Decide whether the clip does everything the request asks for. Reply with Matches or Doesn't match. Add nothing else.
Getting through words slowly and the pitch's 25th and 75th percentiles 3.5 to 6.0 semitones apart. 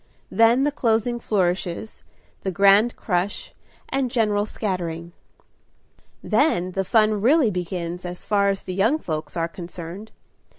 Matches